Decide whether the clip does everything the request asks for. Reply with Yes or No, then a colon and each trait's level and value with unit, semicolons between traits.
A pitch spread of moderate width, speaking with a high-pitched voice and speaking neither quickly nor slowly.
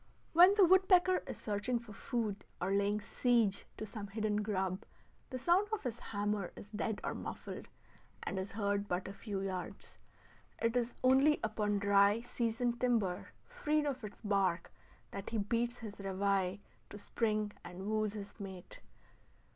Yes: average, 3.2 semitones; high, 210 Hz; average, 160 wpm